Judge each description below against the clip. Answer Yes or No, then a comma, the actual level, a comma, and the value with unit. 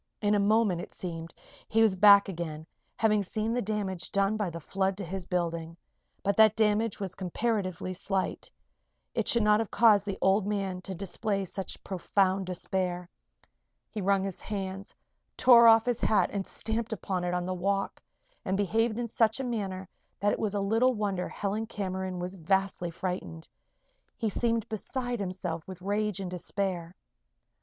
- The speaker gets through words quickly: No, average, 170 wpm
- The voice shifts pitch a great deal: No, average, 2.7 semitones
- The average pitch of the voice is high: Yes, high, 195 Hz